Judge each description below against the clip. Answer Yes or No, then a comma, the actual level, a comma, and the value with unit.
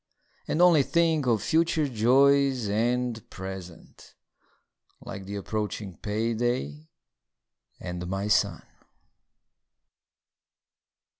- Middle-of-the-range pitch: No, low, 115 Hz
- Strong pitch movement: Yes, wide, 6.0 semitones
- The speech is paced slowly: Yes, slow, 80 wpm